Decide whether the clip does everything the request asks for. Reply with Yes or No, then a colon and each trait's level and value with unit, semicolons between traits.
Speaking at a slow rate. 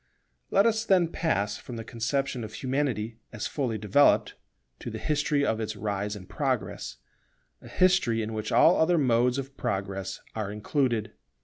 No: average, 165 wpm